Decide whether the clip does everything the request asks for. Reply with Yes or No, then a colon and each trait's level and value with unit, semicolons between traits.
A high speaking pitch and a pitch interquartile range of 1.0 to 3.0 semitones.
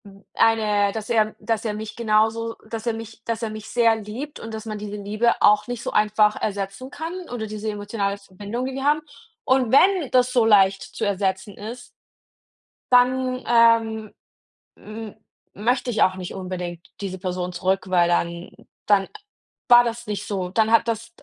Yes: high, 215 Hz; narrow, 2.6 semitones